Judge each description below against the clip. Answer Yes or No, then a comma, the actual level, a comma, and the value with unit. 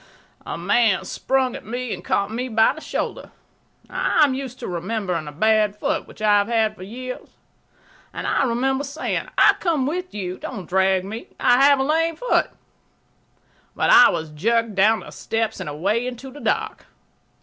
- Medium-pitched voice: No, high, 230 Hz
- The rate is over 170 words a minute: Yes, average, 185 wpm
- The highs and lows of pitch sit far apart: No, average, 4.9 semitones